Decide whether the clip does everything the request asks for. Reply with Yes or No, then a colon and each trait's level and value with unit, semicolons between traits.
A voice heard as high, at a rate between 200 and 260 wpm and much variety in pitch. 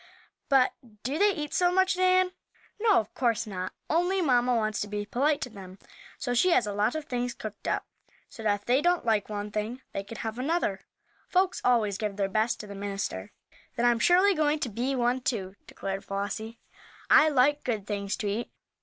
Yes: high, 235 Hz; fast, 205 wpm; wide, 6.3 semitones